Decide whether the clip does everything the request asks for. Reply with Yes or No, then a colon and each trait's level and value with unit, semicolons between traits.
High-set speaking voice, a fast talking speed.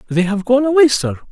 Yes: high, 225 Hz; fast, 230 wpm